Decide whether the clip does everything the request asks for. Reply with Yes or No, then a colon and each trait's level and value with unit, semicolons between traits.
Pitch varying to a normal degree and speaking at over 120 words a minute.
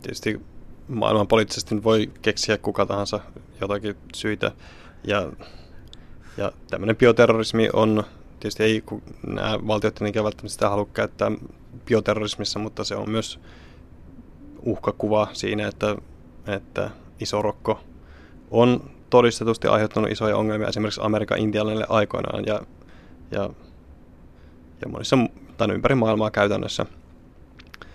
No: average, 4.5 semitones; average, 105 wpm